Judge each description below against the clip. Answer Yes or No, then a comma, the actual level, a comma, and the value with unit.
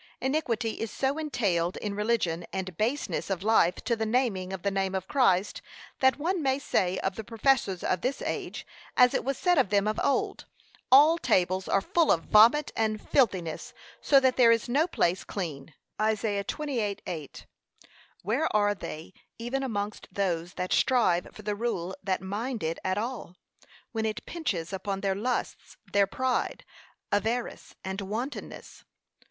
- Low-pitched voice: No, high, 215 Hz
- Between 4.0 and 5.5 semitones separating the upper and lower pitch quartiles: Yes, average, 5.0 semitones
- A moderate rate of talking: Yes, average, 165 wpm